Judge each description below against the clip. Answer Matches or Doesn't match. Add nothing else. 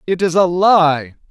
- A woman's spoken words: Doesn't match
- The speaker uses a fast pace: Doesn't match